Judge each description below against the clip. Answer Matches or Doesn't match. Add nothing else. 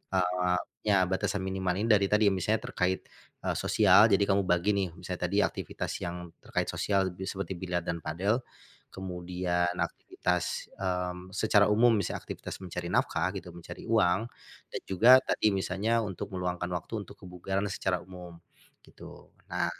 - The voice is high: Doesn't match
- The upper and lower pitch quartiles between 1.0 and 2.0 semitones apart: Matches